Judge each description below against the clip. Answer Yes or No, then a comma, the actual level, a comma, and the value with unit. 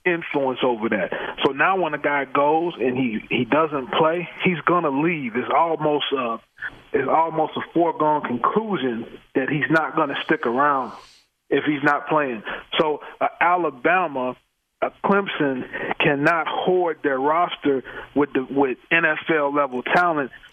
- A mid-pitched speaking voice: Yes, medium, 150 Hz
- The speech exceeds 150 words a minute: No, average, 145 wpm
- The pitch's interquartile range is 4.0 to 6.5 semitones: No, average, 3.4 semitones